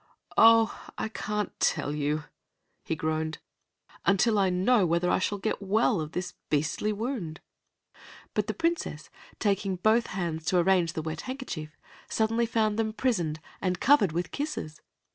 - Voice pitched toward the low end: No, high, 190 Hz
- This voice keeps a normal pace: Yes, average, 150 wpm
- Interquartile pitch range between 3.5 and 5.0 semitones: No, wide, 5.6 semitones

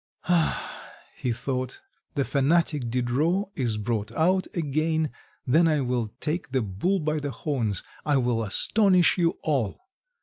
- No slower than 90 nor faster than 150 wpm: Yes, average, 140 wpm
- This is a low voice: No, medium, 145 Hz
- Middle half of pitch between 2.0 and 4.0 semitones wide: No, average, 5.0 semitones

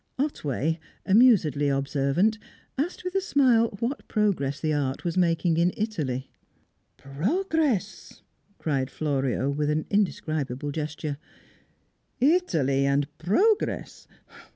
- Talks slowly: Yes, slow, 100 wpm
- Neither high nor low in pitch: Yes, medium, 160 Hz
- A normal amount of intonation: No, wide, 8.2 semitones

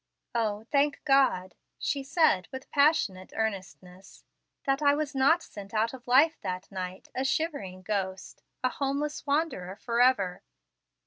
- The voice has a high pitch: Yes, high, 245 Hz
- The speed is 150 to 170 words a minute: No, slow, 135 wpm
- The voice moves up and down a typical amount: No, wide, 6.8 semitones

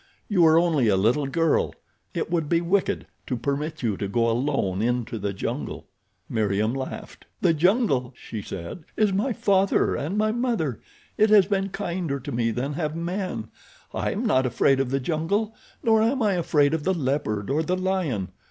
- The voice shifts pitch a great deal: Yes, wide, 7.5 semitones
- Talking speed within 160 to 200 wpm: Yes, average, 180 wpm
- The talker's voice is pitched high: No, medium, 150 Hz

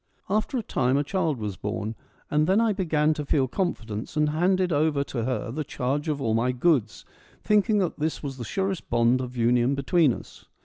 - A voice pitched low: No, medium, 145 Hz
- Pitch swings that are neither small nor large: No, wide, 6.0 semitones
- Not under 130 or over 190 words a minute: No, fast, 205 wpm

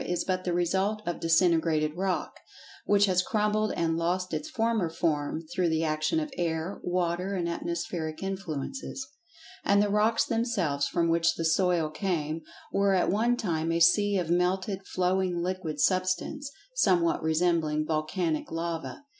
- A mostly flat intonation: No, average, 3.2 semitones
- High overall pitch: No, medium, 180 Hz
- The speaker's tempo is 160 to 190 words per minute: No, average, 150 wpm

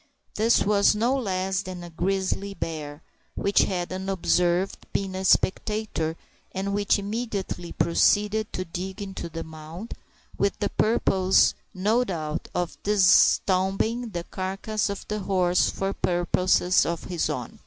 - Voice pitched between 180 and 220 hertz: Yes, high, 190 Hz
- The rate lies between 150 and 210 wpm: No, slow, 135 wpm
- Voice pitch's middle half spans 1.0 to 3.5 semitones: Yes, narrow, 2.6 semitones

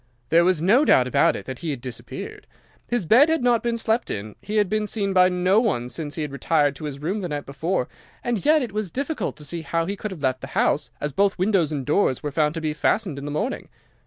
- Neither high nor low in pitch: Yes, medium, 175 Hz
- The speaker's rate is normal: No, fast, 260 wpm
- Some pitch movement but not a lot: No, wide, 6.5 semitones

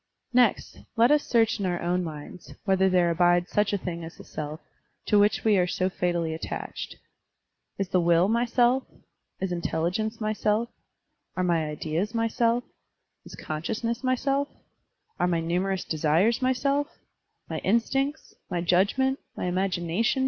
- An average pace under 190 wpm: Yes, average, 160 wpm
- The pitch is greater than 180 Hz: Yes, high, 190 Hz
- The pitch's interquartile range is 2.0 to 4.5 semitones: No, average, 5.1 semitones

